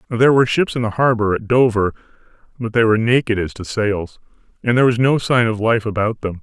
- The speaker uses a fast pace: Yes, fast, 225 wpm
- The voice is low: Yes, low, 115 Hz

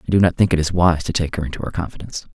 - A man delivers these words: Yes, male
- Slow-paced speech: No, fast, 330 wpm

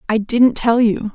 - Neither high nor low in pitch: No, high, 225 Hz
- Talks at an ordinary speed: No, fast, 210 wpm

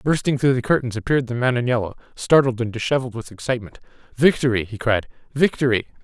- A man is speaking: Yes, male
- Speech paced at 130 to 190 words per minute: Yes, average, 180 wpm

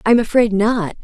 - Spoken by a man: No, female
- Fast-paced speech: No, average, 175 wpm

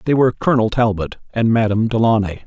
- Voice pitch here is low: Yes, low, 110 Hz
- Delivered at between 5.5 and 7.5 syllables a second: Yes, 6.9 syllables/s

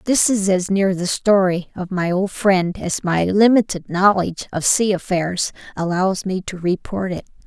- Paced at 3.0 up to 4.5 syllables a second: Yes, 4.4 syllables/s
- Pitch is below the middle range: No, high, 190 Hz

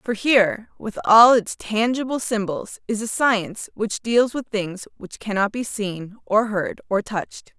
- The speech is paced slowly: No, average, 175 wpm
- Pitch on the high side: Yes, high, 215 Hz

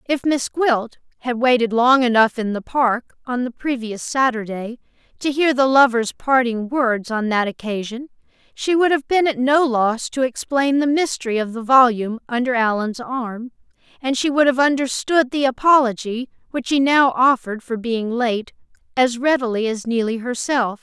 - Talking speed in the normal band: Yes, average, 170 wpm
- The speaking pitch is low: No, very high, 250 Hz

